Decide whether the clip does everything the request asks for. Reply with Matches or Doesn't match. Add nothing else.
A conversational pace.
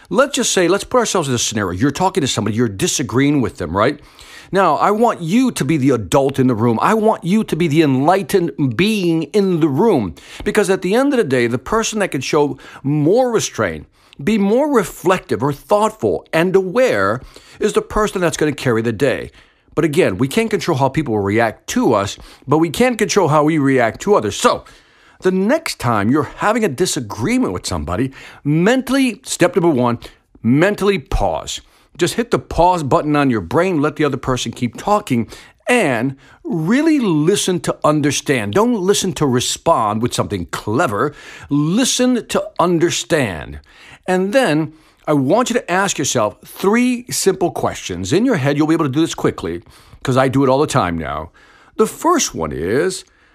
Matches